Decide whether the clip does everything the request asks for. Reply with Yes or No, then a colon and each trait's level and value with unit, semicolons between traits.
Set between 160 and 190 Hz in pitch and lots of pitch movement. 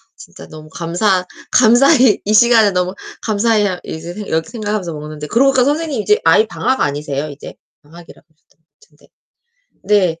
No: high, 200 Hz; wide, 6.2 semitones